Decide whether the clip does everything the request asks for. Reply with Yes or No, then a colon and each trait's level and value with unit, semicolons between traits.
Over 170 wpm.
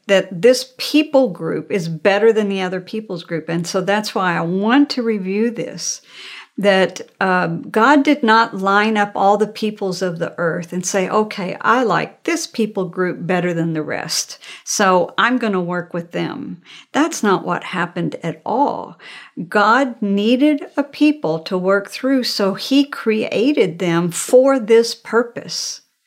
No: average, 165 wpm